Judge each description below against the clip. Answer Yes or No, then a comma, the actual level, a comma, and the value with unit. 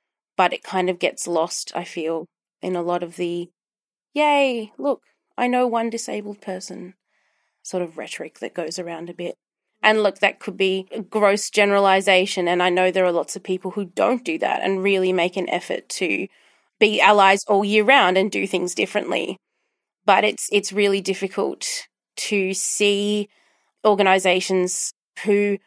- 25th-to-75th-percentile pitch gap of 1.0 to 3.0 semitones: Yes, narrow, 2.4 semitones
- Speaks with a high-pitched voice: Yes, high, 195 Hz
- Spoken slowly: No, average, 170 wpm